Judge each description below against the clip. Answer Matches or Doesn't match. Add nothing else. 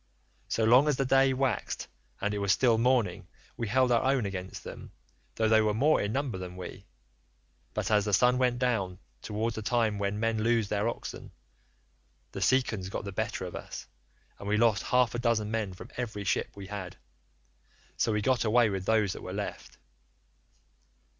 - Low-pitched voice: Matches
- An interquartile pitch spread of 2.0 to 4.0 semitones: Matches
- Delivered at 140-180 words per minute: Doesn't match